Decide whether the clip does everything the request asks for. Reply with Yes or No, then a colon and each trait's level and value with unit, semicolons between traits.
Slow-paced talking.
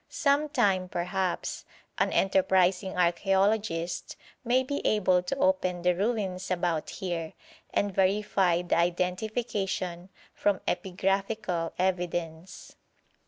Yes: slow, 100 wpm